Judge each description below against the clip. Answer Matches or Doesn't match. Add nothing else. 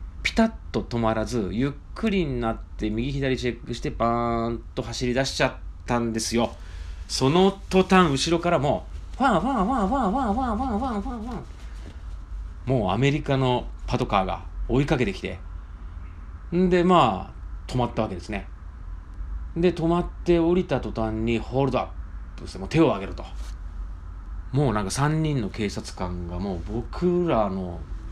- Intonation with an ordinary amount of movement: Doesn't match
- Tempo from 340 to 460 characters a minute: Doesn't match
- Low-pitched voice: Matches